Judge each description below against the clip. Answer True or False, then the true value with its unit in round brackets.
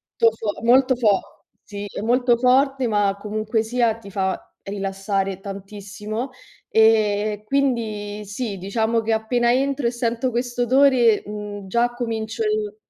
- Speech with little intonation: False (3.0 semitones)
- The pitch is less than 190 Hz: False (225 Hz)